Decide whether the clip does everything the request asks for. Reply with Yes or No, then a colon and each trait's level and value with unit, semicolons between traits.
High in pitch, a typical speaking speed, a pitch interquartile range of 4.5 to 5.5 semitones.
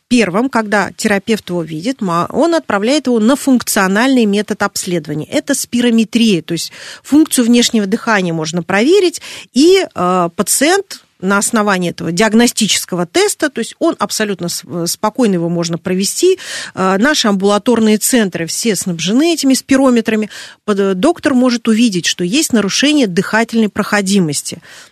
Yes: high, 220 Hz; average, 125 wpm; average, 4.8 semitones